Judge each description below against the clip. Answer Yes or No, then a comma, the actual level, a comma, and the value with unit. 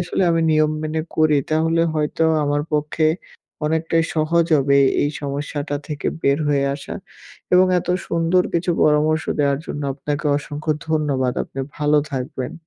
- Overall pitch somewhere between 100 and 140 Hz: No, medium, 150 Hz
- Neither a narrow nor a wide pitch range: No, narrow, 1.9 semitones